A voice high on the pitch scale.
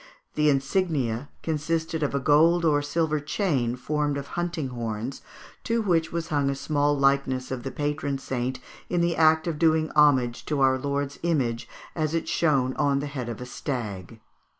No: medium, 145 Hz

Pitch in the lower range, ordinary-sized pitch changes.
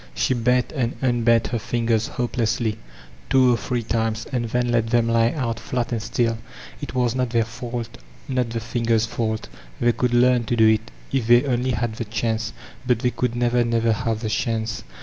No: low, 115 Hz; narrow, 1.4 semitones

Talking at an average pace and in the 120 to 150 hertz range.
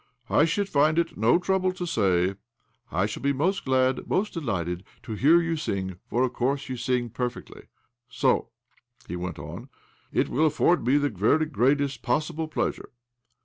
Yes: average, 190 wpm; low, 135 Hz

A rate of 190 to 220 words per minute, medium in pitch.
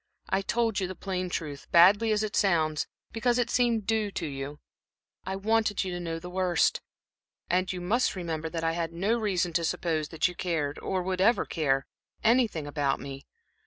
Yes: average, 195 wpm; medium, 180 Hz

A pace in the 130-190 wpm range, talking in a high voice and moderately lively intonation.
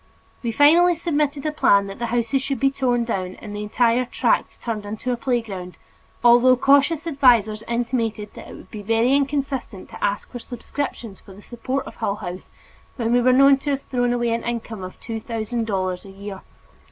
No: average, 200 wpm; high, 240 Hz; average, 4.2 semitones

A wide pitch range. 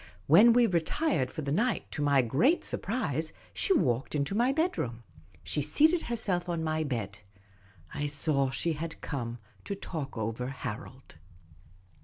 Yes: wide, 8.0 semitones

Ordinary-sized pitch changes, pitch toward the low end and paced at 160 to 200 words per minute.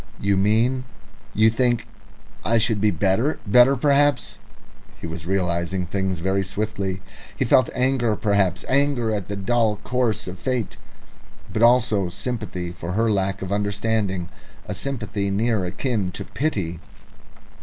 No: average, 4.0 semitones; low, 105 Hz; average, 145 wpm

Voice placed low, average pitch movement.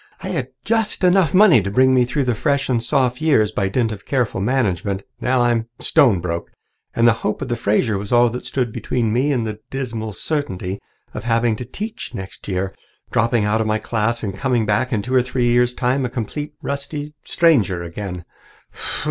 Yes: low, 120 Hz; average, 3.7 semitones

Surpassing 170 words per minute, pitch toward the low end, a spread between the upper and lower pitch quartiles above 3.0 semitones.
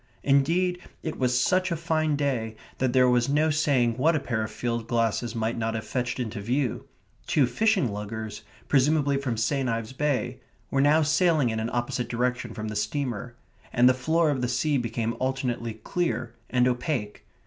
Yes: average, 180 wpm; low, 125 Hz; average, 4.0 semitones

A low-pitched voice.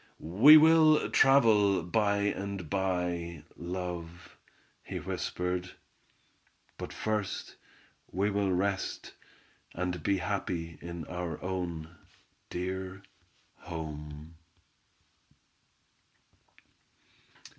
Yes: very low, 90 Hz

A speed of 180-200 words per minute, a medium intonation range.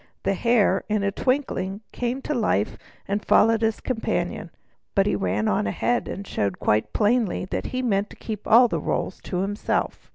Yes: average, 185 wpm; average, 3.7 semitones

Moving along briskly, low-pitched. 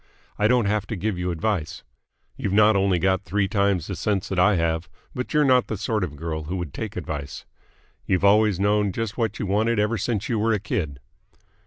Yes: fast, 215 wpm; low, 100 Hz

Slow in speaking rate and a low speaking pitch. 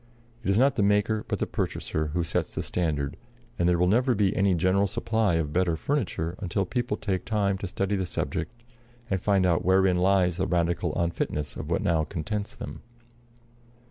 No: average, 190 wpm; very low, 95 Hz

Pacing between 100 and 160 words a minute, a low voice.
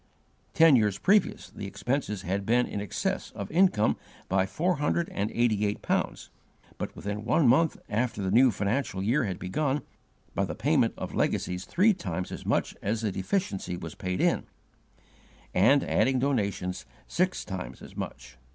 No: average, 170 wpm; low, 110 Hz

